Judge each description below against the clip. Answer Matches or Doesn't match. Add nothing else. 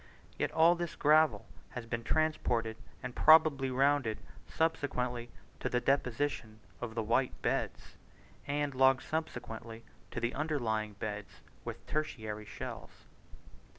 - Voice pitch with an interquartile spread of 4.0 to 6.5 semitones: Matches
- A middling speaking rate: Doesn't match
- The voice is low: Matches